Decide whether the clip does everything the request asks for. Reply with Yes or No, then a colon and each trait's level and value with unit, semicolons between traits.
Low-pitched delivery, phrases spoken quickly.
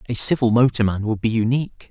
No: low, 115 Hz; average, 190 wpm